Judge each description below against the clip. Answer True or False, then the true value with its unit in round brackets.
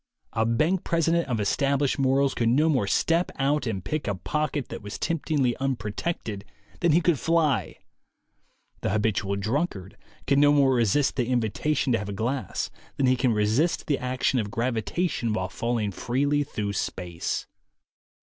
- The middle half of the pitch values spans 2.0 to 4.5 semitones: False (5.4 semitones)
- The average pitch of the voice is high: False (130 Hz)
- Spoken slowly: False (165 wpm)